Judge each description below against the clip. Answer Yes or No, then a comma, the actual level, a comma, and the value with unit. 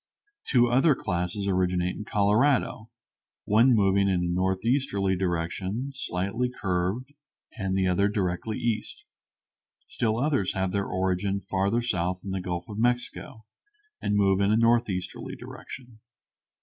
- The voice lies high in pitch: No, low, 100 Hz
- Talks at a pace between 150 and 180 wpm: No, slow, 135 wpm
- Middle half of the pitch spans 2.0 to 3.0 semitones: No, average, 3.9 semitones